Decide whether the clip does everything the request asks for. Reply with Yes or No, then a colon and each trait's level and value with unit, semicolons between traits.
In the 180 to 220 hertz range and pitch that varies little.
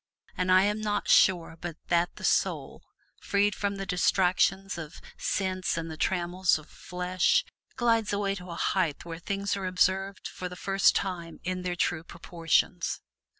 Yes: medium, 185 Hz; narrow, 2.3 semitones